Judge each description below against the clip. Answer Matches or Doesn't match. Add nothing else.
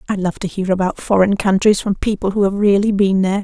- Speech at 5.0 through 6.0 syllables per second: Doesn't match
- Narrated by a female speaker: Matches